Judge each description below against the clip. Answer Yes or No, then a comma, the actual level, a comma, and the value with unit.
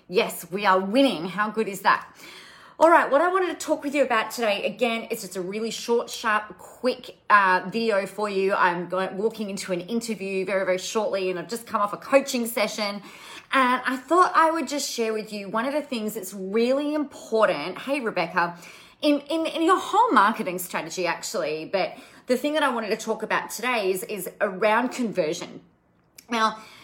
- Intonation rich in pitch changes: Yes, wide, 5.8 semitones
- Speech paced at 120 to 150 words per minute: No, average, 200 wpm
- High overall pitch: Yes, high, 220 Hz